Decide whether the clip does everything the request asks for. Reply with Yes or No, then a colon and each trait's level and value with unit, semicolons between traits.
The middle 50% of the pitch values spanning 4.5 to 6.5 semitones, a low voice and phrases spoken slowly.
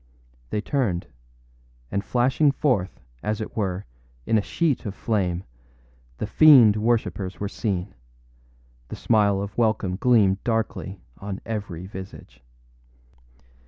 No: average, 3.3 semitones; low, 105 Hz; slow, 125 wpm